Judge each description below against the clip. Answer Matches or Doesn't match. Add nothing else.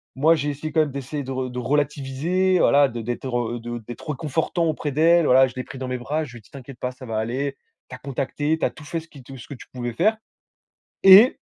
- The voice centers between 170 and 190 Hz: Doesn't match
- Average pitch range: Matches